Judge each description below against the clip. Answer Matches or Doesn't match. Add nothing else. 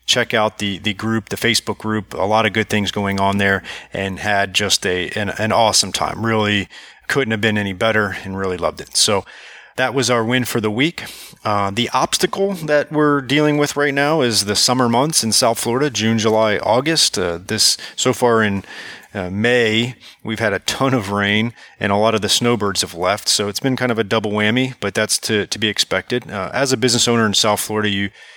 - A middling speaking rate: Doesn't match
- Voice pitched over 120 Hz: Doesn't match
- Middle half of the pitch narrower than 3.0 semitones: Doesn't match